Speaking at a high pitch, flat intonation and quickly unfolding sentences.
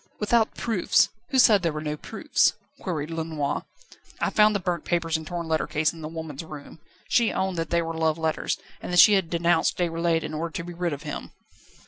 No: medium, 165 Hz; narrow, 2.0 semitones; fast, 215 wpm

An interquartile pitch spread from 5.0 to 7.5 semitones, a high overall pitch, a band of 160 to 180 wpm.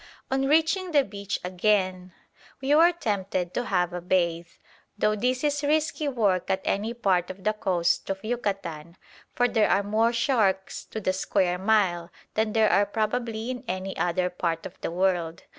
No: average, 4.5 semitones; high, 200 Hz; average, 175 wpm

